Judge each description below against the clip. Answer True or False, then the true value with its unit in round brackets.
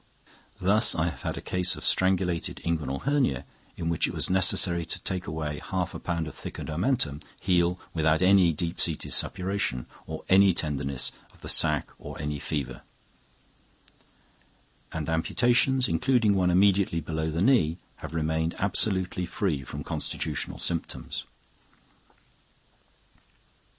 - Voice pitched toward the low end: True (85 Hz)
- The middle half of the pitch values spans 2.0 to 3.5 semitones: True (3.2 semitones)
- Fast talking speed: False (135 wpm)